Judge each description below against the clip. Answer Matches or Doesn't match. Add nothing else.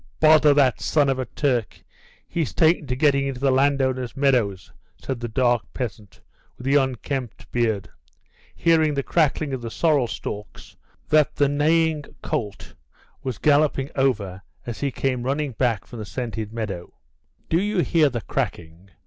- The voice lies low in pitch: Matches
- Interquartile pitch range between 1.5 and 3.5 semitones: Doesn't match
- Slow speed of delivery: Doesn't match